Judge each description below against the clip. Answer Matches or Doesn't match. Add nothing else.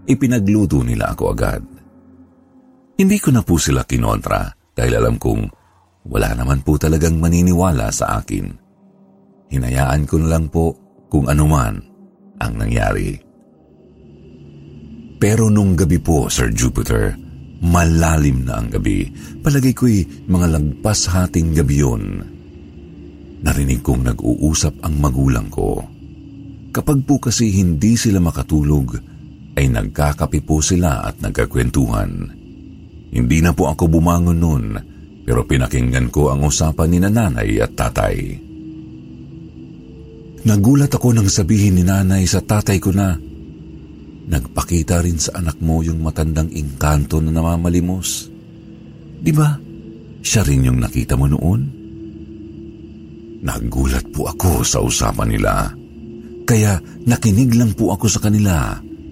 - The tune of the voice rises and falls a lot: Matches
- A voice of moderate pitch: Doesn't match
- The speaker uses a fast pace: Doesn't match